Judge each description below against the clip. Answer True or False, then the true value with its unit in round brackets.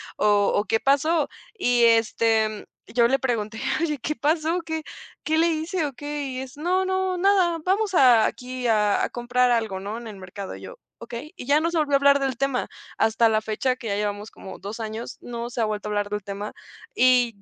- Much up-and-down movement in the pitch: True (5.8 semitones)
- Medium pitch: False (245 Hz)